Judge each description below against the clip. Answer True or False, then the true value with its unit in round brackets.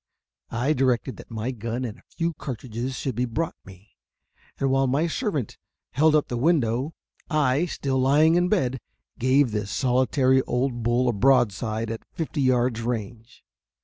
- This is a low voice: True (130 Hz)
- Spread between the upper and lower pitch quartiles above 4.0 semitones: False (3.3 semitones)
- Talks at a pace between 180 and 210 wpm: False (160 wpm)